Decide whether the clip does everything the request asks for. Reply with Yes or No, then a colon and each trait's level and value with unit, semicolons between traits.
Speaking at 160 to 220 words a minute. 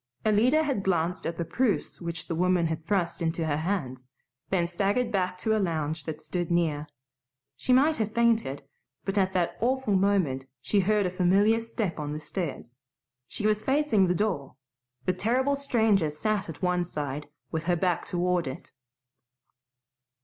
Yes: average, 170 wpm